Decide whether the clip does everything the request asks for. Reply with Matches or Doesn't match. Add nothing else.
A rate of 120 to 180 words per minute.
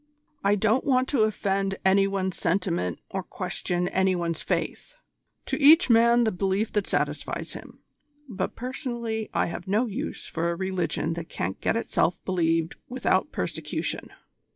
Matches